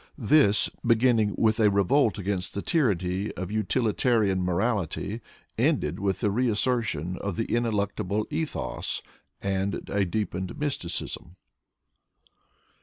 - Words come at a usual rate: No, slow, 110 wpm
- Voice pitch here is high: No, low, 105 Hz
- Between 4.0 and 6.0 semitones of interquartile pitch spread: No, average, 3.6 semitones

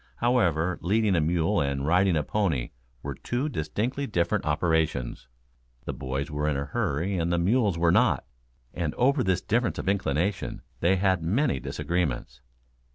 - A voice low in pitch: Yes, very low, 85 Hz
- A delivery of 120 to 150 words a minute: No, average, 160 wpm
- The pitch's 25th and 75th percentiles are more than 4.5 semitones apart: Yes, average, 5.1 semitones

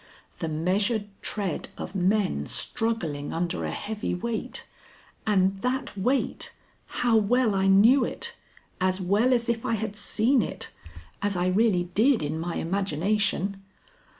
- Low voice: No, high, 205 Hz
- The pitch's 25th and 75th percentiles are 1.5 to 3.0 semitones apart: No, average, 3.8 semitones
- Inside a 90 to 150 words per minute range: Yes, average, 140 wpm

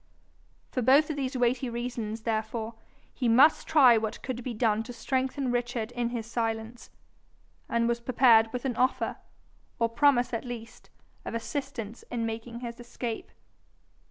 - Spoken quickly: No, average, 155 wpm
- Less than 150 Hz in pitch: No, high, 240 Hz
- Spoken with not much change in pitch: Yes, narrow, 2.0 semitones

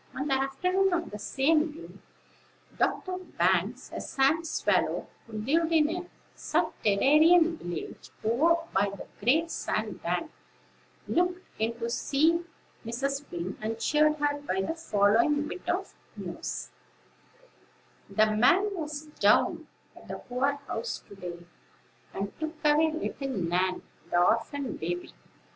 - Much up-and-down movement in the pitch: Yes, wide, 7.1 semitones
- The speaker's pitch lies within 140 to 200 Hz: No, very high, 280 Hz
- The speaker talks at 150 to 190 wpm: No, slow, 135 wpm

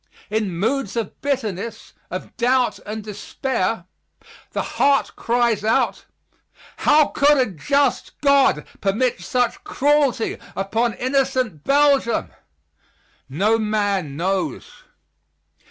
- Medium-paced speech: No, slow, 100 wpm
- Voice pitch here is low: No, high, 230 Hz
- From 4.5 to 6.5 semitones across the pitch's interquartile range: Yes, average, 5.2 semitones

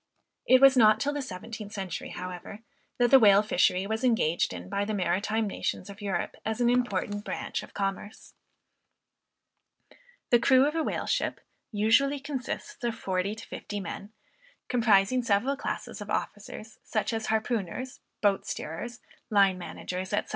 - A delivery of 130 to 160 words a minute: Yes, average, 155 wpm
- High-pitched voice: Yes, high, 215 Hz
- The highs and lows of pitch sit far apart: No, average, 3.7 semitones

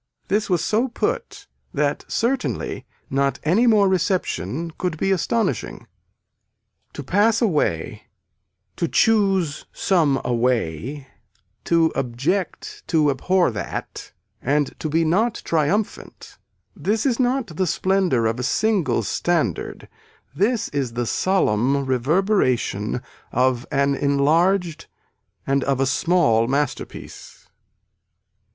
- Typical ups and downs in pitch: No, wide, 6.7 semitones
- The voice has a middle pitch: Yes, medium, 160 Hz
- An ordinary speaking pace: No, slow, 110 wpm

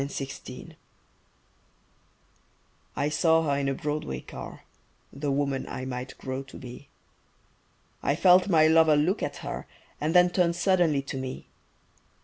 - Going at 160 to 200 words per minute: No, average, 145 wpm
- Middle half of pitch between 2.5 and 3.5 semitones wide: Yes, average, 3.2 semitones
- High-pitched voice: No, medium, 145 Hz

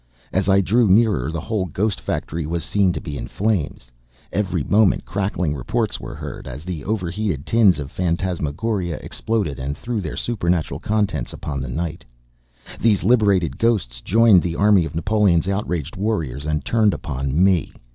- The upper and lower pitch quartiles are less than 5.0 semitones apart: No, average, 5.3 semitones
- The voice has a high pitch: No, very low, 90 Hz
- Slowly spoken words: No, average, 165 wpm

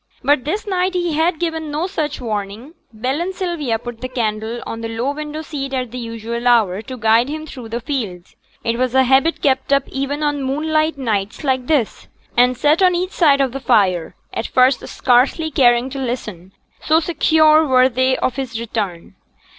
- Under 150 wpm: No, average, 195 wpm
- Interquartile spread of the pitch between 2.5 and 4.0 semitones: No, average, 4.7 semitones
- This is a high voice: Yes, very high, 260 Hz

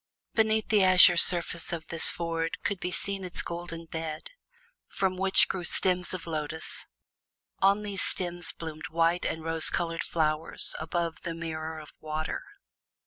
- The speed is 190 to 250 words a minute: No, average, 150 wpm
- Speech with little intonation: Yes, narrow, 2.2 semitones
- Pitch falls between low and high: Yes, medium, 170 Hz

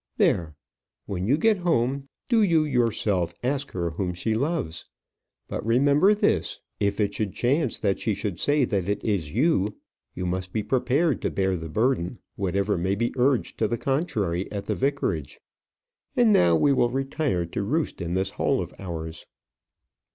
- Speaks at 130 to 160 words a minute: No, average, 175 wpm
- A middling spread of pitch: No, wide, 7.1 semitones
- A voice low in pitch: Yes, low, 110 Hz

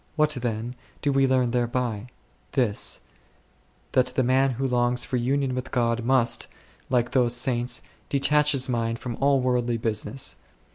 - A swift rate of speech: No, average, 160 wpm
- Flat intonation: Yes, narrow, 1.9 semitones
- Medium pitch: No, low, 125 Hz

